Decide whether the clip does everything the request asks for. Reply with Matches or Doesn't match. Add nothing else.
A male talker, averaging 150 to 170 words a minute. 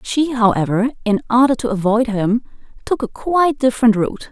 Doesn't match